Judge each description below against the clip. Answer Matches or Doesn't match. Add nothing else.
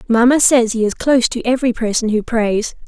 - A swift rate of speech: Matches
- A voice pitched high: Matches